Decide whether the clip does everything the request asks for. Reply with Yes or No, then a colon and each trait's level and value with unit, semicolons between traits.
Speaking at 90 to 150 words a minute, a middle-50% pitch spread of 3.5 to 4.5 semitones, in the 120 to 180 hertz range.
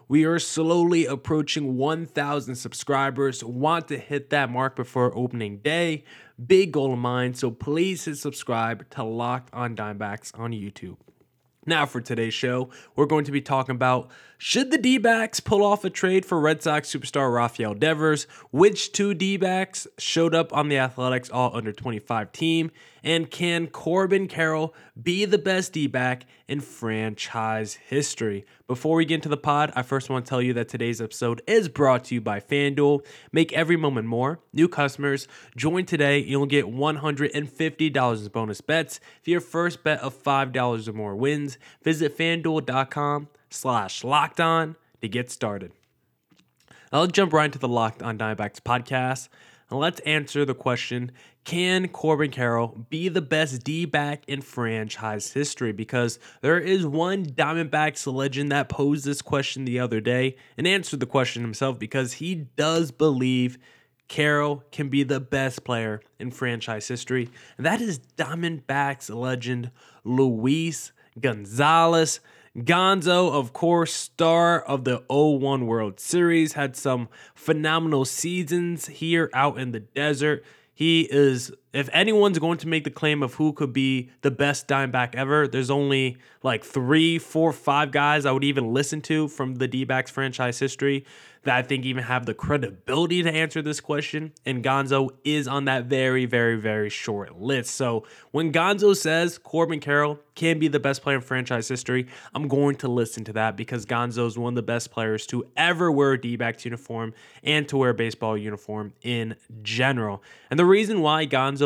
No: average, 165 wpm; average, 4.1 semitones; medium, 140 Hz